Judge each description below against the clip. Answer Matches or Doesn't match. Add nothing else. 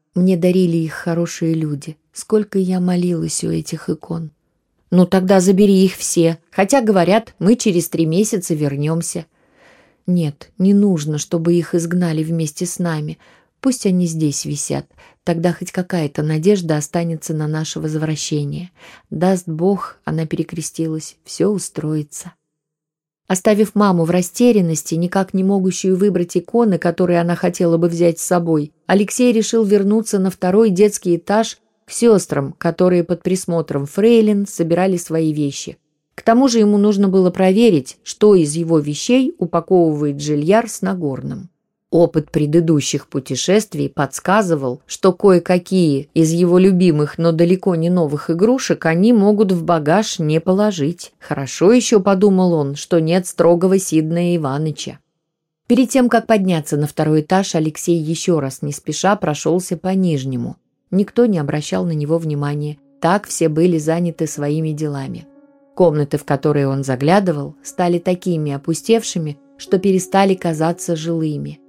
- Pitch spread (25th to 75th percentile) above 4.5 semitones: Doesn't match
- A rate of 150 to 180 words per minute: Doesn't match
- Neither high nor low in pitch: Matches